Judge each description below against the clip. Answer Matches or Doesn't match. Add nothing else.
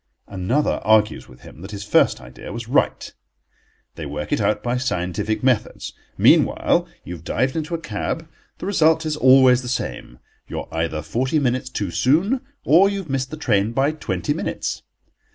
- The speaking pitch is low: Matches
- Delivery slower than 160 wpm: Doesn't match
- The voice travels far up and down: Matches